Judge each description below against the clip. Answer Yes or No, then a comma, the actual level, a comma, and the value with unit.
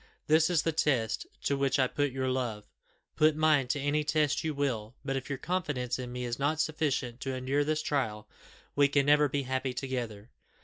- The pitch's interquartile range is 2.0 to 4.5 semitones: Yes, average, 2.8 semitones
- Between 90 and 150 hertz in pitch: Yes, low, 135 Hz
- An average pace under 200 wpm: No, fast, 205 wpm